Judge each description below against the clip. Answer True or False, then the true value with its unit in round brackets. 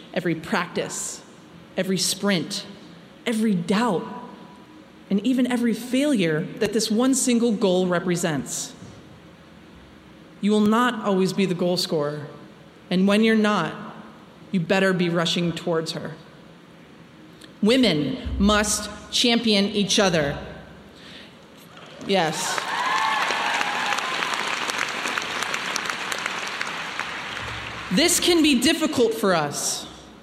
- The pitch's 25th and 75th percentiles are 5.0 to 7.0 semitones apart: False (4.2 semitones)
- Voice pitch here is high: True (200 Hz)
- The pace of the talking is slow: True (90 wpm)